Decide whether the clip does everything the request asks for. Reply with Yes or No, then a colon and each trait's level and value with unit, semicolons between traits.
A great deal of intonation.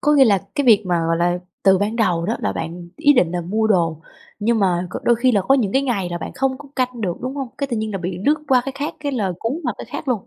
Yes: wide, 6.4 semitones